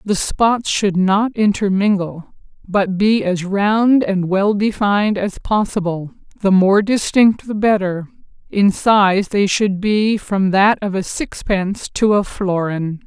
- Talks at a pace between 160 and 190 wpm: No, average, 145 wpm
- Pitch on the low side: No, high, 200 Hz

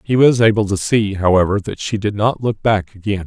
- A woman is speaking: No, male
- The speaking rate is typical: No, fast, 240 wpm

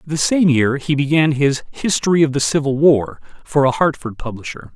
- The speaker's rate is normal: Yes, average, 190 wpm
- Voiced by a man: Yes, male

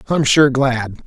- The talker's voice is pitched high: No, low, 130 Hz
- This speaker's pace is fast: No, average, 170 wpm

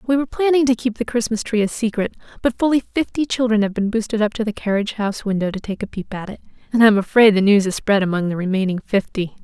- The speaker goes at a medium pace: No, fast, 260 wpm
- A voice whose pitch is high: Yes, high, 215 Hz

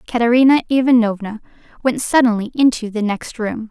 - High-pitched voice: Yes, high, 230 Hz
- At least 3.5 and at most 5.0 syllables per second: No, 5.6 syllables/s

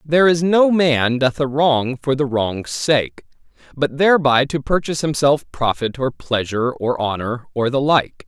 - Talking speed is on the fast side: No, average, 175 wpm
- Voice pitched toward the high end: No, medium, 140 Hz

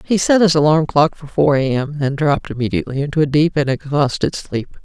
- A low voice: No, medium, 145 Hz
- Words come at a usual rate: No, fast, 225 wpm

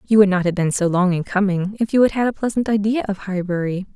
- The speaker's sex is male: No, female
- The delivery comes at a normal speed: No, fast, 275 wpm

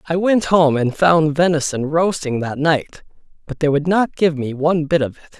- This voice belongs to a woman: No, male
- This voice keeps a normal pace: No, fast, 210 wpm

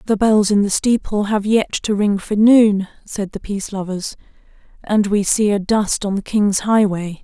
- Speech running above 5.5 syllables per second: No, 4.5 syllables/s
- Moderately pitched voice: No, high, 205 Hz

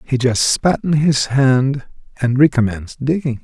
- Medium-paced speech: Yes, average, 155 wpm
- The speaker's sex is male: Yes, male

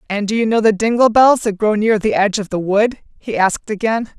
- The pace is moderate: No, fast, 260 wpm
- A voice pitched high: Yes, high, 215 Hz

